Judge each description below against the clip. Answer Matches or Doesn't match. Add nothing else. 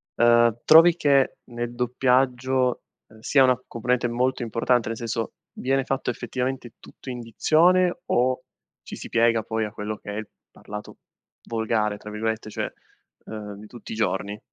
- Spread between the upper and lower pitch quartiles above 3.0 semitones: Doesn't match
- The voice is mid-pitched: Doesn't match